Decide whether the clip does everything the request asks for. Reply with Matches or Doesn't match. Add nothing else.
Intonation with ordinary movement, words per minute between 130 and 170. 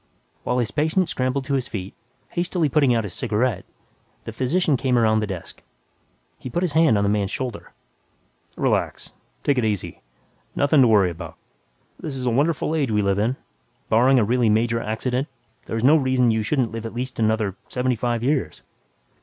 Doesn't match